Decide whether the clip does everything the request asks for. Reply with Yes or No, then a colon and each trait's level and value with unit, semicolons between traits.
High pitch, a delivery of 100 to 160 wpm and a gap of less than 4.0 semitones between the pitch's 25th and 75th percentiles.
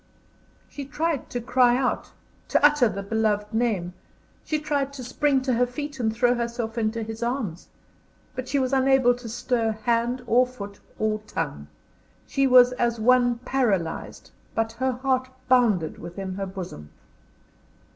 Yes: high, 240 Hz; average, 155 wpm; average, 3.0 semitones